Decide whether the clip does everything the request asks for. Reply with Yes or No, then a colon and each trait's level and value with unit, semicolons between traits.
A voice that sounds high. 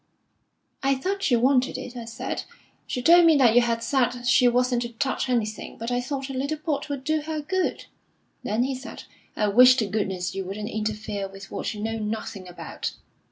Yes: high, 245 Hz